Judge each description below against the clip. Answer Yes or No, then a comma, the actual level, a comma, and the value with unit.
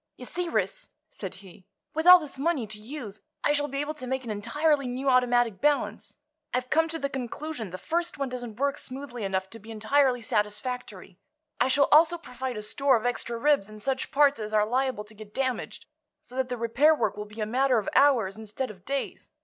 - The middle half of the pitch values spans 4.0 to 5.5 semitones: Yes, average, 4.7 semitones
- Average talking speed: No, fast, 215 wpm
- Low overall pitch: No, very high, 250 Hz